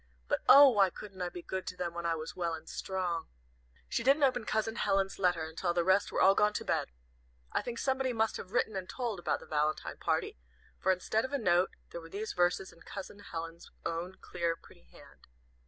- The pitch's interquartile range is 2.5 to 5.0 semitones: Yes, average, 4.2 semitones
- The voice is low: No, high, 190 Hz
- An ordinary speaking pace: No, fast, 220 wpm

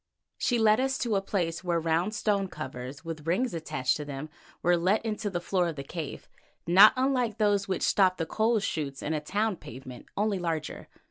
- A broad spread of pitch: No, average, 5.0 semitones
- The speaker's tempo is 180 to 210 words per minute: Yes, average, 200 wpm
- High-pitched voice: No, medium, 180 Hz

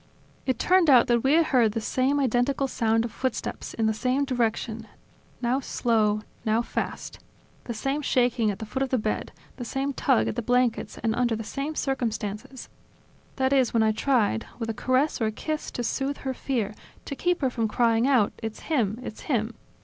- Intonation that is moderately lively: Yes, average, 3.2 semitones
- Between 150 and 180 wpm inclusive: No, average, 200 wpm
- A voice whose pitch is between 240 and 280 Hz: Yes, high, 245 Hz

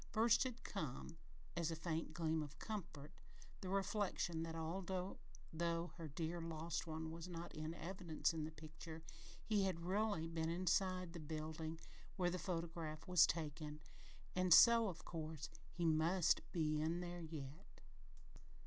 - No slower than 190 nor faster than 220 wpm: No, average, 150 wpm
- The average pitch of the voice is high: No, medium, 165 Hz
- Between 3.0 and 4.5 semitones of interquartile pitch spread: No, narrow, 2.4 semitones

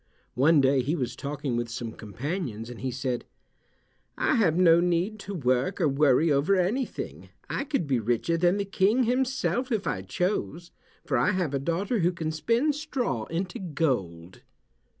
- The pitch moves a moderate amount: No, wide, 7.2 semitones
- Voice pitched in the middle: Yes, medium, 165 Hz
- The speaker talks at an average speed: Yes, average, 170 wpm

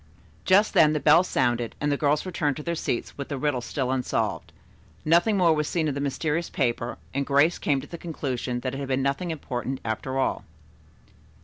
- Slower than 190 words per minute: No, fast, 205 wpm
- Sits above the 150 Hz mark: No, medium, 145 Hz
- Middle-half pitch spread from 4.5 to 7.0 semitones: No, average, 3.3 semitones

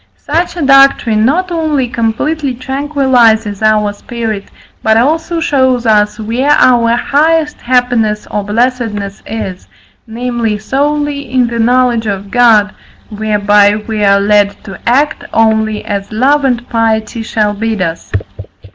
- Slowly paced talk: Yes, slow, 130 wpm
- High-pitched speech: Yes, high, 230 Hz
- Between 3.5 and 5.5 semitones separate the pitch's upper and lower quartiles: Yes, average, 4.0 semitones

